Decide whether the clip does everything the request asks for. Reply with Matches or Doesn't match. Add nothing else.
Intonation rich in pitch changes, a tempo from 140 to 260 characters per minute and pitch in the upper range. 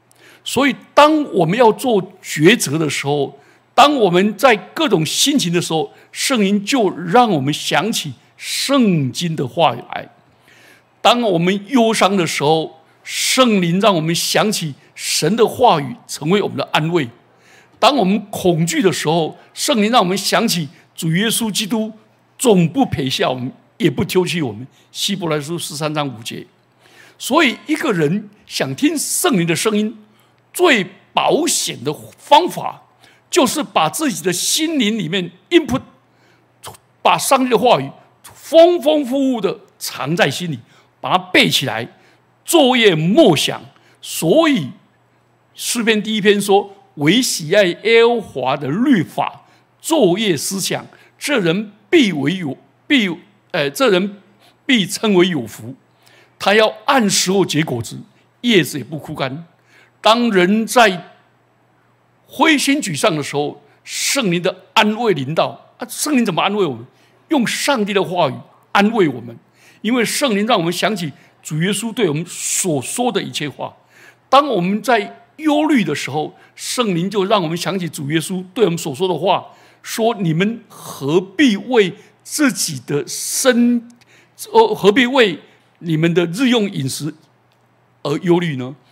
Matches